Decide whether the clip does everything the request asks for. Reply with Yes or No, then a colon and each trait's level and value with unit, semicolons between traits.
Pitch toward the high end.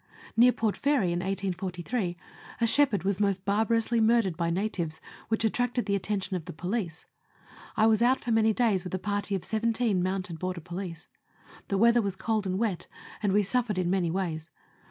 Yes: high, 200 Hz